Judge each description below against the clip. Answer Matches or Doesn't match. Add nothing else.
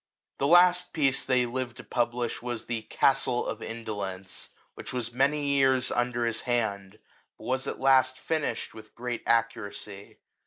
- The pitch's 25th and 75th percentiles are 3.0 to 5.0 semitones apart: Doesn't match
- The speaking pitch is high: Doesn't match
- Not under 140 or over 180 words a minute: Matches